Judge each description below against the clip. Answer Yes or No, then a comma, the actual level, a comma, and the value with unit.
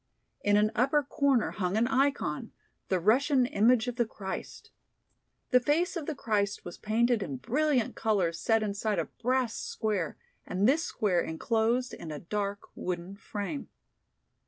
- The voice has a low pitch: No, high, 220 Hz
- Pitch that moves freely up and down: No, average, 4.3 semitones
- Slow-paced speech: No, average, 155 wpm